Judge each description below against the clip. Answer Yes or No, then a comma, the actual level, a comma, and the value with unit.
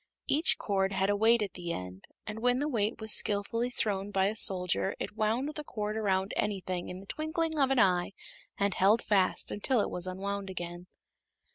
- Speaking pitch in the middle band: No, high, 205 Hz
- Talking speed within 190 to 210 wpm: Yes, average, 195 wpm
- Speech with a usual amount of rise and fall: Yes, average, 3.3 semitones